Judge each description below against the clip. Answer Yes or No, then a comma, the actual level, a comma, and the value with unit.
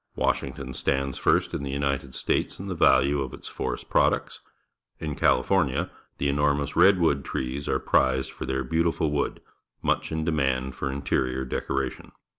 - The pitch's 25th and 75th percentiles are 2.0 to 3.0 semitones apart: Yes, narrow, 2.4 semitones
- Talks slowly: No, average, 160 wpm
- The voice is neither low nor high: No, very low, 70 Hz